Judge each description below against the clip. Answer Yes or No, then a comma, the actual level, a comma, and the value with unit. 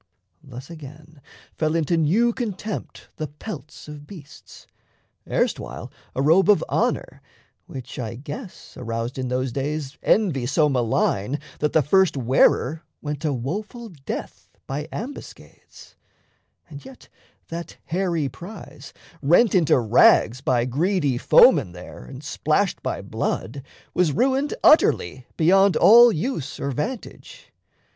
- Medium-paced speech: No, slow, 125 wpm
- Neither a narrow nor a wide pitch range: No, wide, 6.3 semitones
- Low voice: No, medium, 150 Hz